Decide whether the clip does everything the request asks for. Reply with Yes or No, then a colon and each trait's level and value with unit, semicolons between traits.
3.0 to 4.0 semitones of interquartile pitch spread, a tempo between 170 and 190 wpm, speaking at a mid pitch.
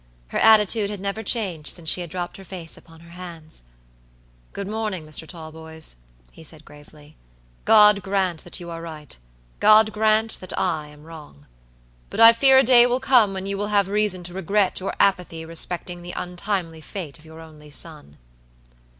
No: average, 4.4 semitones; average, 180 wpm; medium, 180 Hz